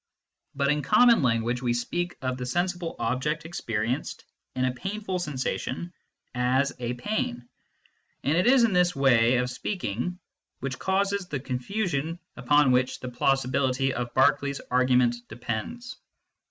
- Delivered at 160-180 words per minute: No, average, 140 wpm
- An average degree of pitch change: No, wide, 5.9 semitones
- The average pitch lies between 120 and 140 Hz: Yes, low, 135 Hz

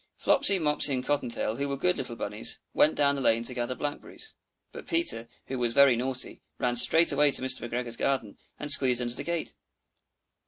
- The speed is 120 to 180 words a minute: No, average, 200 wpm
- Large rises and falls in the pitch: No, average, 3.5 semitones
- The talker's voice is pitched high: No, low, 130 Hz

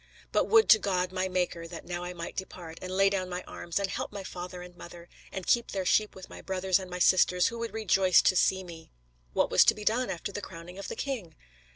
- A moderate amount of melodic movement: No, narrow, 1.9 semitones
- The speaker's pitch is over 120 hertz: Yes, medium, 185 Hz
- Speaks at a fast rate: Yes, fast, 250 wpm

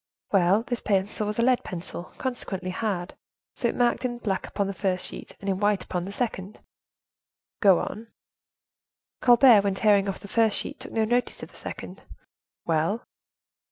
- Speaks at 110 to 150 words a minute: No, average, 175 wpm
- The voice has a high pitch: Yes, high, 205 Hz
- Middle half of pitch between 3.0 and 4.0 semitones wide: Yes, average, 3.5 semitones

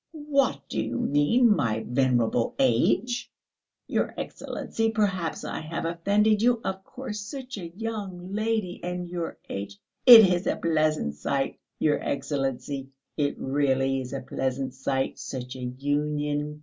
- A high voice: No, medium, 150 Hz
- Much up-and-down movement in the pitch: Yes, wide, 7.3 semitones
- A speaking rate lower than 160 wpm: Yes, average, 140 wpm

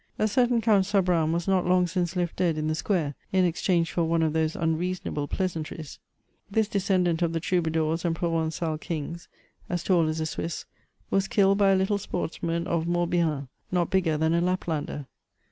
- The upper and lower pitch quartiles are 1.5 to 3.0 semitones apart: Yes, narrow, 2.4 semitones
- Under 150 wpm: No, average, 180 wpm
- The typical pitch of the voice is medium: Yes, medium, 170 Hz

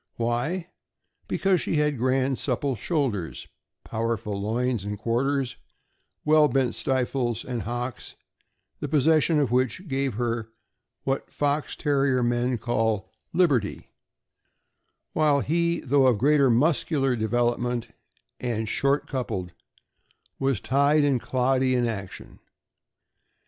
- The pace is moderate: No, slow, 110 wpm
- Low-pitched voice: Yes, low, 130 Hz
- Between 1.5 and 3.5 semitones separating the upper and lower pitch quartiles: Yes, average, 3.2 semitones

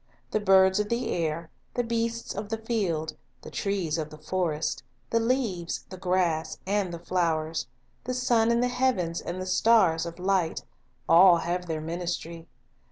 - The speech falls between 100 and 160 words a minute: No, average, 170 wpm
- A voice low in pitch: No, medium, 185 Hz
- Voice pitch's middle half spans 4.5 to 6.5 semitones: Yes, average, 5.1 semitones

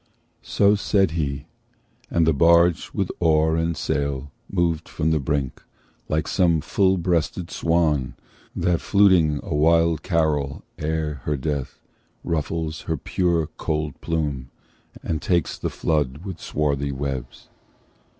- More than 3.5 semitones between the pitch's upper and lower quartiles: No, narrow, 2.5 semitones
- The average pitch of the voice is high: No, very low, 80 Hz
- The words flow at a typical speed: No, slow, 130 wpm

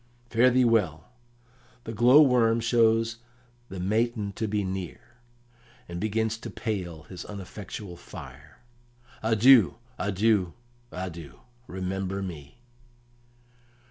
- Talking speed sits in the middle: No, slow, 105 wpm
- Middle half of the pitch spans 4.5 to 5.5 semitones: No, average, 3.8 semitones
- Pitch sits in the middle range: No, low, 105 Hz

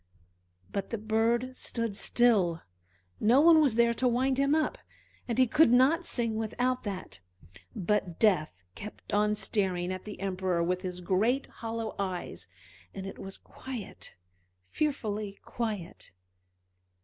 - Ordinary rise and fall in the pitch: Yes, average, 4.3 semitones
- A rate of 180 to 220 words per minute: No, slow, 135 wpm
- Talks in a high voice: Yes, high, 220 Hz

